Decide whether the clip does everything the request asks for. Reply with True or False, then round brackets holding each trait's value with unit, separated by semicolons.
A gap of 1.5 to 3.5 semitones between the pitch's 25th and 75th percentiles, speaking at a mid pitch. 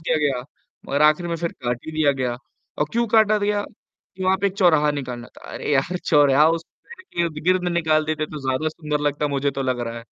False (3.9 semitones; 155 Hz)